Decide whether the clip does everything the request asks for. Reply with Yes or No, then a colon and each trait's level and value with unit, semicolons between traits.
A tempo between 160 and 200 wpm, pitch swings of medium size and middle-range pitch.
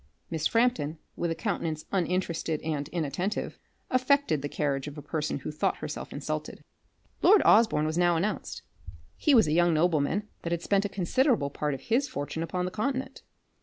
No: average, 175 wpm; wide, 5.7 semitones; medium, 170 Hz